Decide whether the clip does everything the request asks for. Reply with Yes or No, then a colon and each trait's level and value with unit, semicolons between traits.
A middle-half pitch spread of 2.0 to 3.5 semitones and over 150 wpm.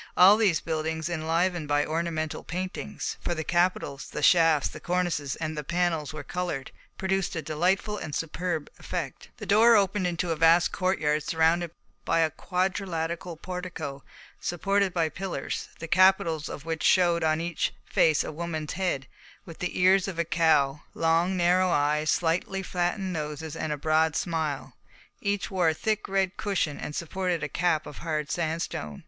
Yes: narrow, 2.6 semitones; average, 165 wpm